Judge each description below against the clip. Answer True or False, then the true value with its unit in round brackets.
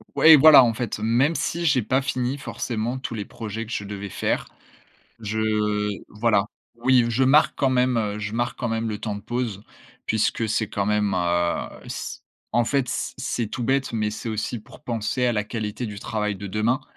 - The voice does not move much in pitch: False (3.0 semitones)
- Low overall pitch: True (115 Hz)